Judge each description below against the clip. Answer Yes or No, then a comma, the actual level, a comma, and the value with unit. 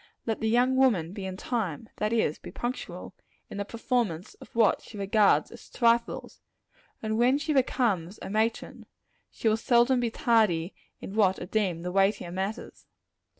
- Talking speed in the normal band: Yes, average, 170 wpm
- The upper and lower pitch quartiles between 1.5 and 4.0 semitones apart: Yes, average, 3.6 semitones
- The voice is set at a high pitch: Yes, high, 220 Hz